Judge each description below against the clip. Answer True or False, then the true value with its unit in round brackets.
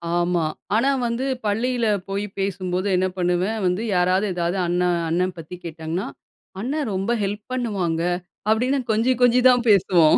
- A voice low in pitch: False (190 Hz)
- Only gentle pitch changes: False (4.1 semitones)